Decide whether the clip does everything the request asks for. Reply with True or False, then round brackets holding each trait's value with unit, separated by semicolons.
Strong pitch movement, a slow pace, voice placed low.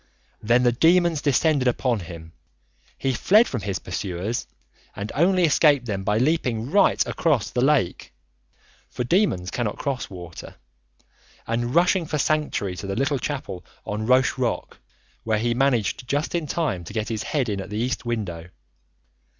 False (6.0 semitones; 165 wpm; 120 Hz)